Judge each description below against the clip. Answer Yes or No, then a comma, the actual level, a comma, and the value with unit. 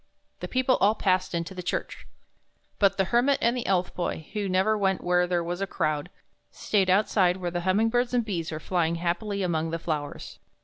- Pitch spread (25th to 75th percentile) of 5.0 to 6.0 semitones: No, average, 3.3 semitones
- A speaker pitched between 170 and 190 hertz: Yes, medium, 185 Hz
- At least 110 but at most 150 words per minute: No, fast, 205 wpm